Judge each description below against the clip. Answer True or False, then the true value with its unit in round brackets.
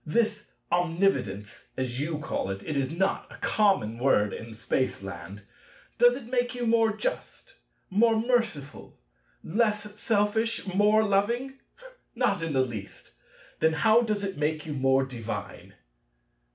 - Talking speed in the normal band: False (130 wpm)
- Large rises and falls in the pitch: True (8.9 semitones)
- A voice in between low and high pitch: False (195 Hz)